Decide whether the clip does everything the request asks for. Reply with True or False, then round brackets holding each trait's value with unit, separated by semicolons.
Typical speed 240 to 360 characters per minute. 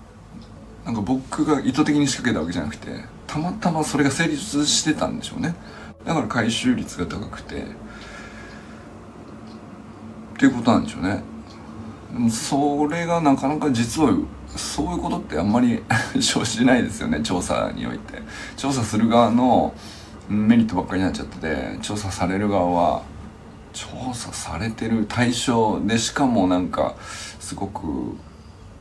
True (300 characters per minute)